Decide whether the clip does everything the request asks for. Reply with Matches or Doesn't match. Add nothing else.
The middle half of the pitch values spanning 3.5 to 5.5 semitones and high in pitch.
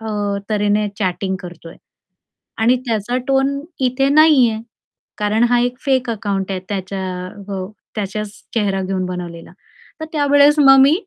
Matches